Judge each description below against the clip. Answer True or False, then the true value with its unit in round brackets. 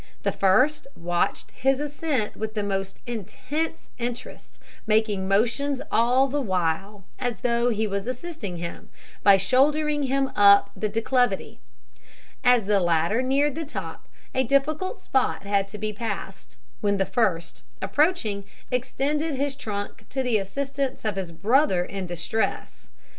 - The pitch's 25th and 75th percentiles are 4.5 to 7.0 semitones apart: True (5.5 semitones)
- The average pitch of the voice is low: False (225 Hz)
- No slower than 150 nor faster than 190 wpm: False (140 wpm)